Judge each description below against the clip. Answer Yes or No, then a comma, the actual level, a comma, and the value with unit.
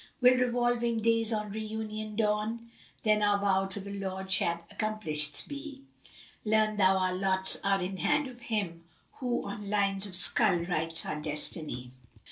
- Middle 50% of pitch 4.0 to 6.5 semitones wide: No, average, 2.8 semitones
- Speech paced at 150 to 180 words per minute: Yes, average, 170 wpm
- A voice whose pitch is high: Yes, high, 205 Hz